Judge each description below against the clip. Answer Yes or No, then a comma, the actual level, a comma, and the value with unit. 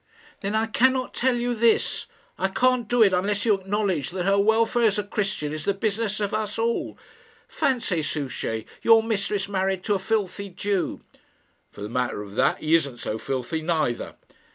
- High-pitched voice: Yes, high, 200 Hz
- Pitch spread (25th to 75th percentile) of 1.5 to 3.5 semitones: No, average, 5.1 semitones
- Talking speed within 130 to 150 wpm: No, average, 180 wpm